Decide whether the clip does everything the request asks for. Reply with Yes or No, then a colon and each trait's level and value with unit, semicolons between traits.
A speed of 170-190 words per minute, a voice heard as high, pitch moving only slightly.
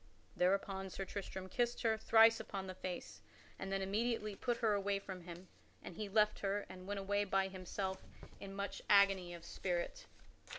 Yes: average, 175 wpm; high, 195 Hz; narrow, 1.6 semitones